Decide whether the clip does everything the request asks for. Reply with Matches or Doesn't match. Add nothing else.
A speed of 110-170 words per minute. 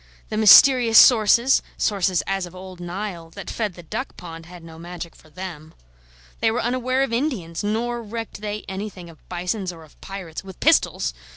Doesn't match